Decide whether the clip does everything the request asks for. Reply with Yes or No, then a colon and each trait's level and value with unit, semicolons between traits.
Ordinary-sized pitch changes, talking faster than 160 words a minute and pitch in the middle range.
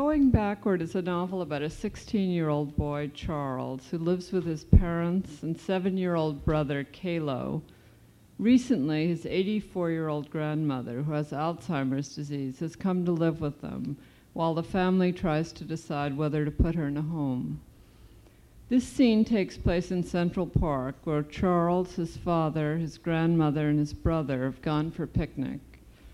No: average, 3.4 semitones; average, 150 wpm; medium, 160 Hz